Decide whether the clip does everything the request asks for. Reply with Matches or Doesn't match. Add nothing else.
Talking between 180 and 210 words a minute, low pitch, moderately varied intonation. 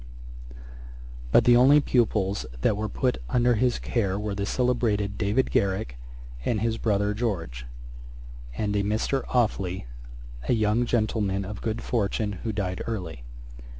Doesn't match